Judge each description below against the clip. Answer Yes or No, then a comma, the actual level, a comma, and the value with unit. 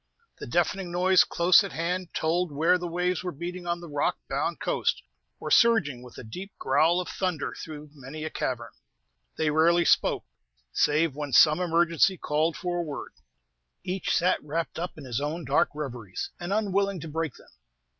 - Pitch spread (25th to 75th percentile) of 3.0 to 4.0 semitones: Yes, average, 3.3 semitones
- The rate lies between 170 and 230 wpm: Yes, average, 180 wpm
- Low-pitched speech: No, medium, 165 Hz